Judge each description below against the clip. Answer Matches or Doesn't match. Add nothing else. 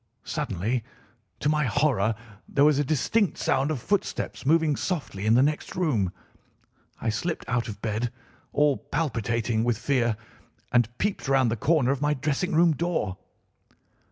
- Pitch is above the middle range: Doesn't match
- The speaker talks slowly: Doesn't match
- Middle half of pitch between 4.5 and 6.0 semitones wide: Matches